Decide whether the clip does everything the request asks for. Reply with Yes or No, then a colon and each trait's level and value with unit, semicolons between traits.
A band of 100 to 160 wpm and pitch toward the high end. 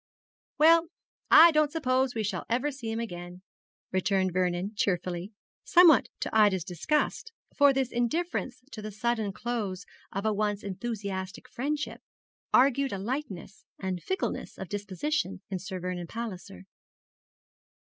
Yes: slow, 135 wpm; high, 215 Hz